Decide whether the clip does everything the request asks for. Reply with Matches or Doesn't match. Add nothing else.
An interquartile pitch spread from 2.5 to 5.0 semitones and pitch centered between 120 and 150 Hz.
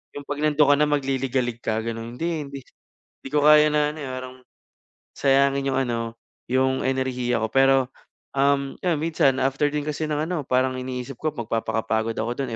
Matches